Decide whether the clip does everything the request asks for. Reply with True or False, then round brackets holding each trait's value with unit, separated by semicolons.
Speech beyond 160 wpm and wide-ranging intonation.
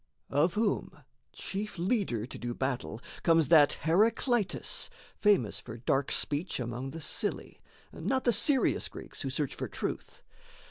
False (140 wpm; 8.3 semitones)